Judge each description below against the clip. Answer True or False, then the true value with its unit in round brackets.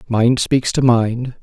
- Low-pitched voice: True (120 Hz)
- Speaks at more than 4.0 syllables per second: False (3.2 syllables/s)